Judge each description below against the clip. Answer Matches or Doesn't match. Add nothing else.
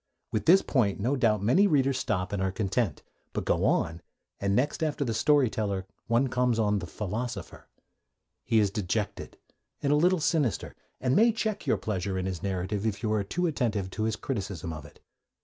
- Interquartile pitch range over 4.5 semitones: Matches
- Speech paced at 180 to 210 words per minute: Matches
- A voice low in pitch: Matches